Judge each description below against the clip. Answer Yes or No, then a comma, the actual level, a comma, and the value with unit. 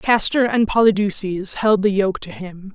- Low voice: No, high, 200 Hz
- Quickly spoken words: No, average, 175 wpm